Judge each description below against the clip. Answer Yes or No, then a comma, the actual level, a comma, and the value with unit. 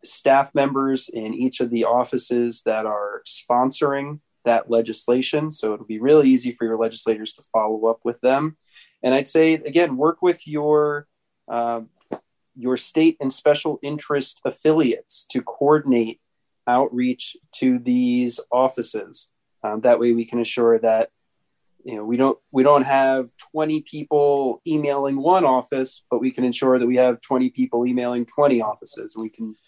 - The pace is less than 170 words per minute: Yes, average, 160 wpm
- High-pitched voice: No, low, 130 Hz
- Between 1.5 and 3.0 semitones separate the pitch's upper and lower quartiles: No, average, 3.7 semitones